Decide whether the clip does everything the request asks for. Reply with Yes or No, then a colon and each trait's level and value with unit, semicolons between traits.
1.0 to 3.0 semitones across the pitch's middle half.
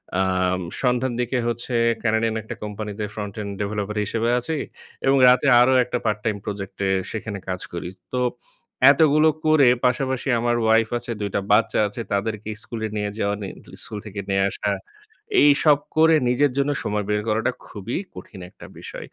No: average, 3.4 semitones